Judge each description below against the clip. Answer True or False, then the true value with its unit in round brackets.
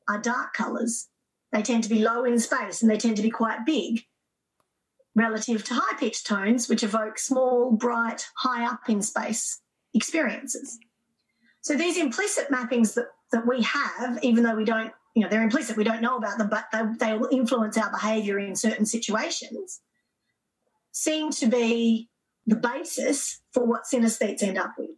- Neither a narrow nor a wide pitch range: False (2.2 semitones)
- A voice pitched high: True (230 Hz)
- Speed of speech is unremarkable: True (175 wpm)